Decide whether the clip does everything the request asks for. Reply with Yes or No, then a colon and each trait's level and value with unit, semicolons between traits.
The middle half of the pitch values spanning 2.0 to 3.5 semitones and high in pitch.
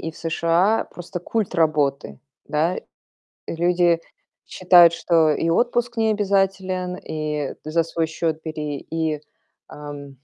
No: average, 3.0 semitones; medium, 165 Hz